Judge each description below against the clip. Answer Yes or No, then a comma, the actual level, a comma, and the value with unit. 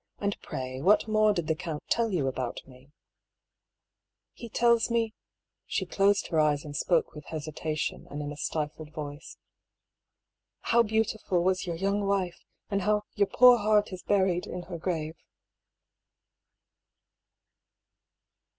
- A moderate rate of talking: Yes, average, 155 wpm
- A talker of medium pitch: Yes, medium, 180 Hz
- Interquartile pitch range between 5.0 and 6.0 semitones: Yes, average, 5.3 semitones